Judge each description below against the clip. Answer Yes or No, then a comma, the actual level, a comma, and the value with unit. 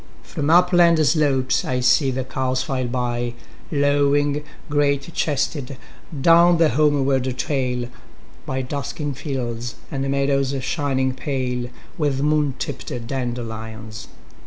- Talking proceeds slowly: Yes, slow, 100 wpm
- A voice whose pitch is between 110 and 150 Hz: Yes, low, 135 Hz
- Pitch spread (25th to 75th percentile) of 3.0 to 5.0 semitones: No, narrow, 2.5 semitones